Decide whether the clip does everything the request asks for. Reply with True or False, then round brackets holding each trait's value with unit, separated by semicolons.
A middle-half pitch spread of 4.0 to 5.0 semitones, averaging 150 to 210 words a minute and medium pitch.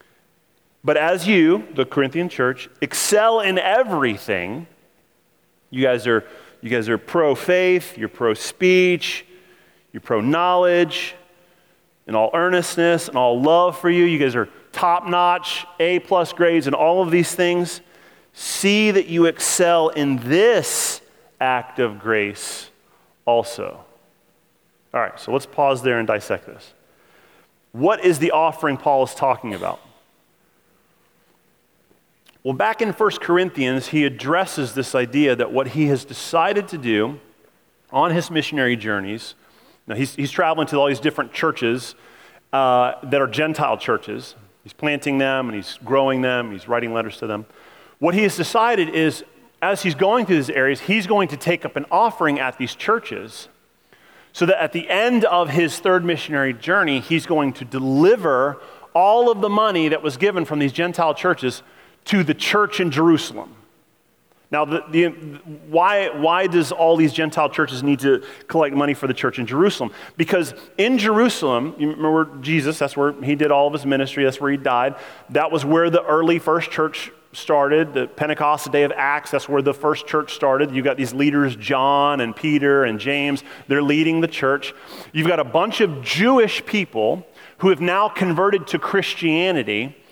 True (4.5 semitones; 165 wpm; 155 Hz)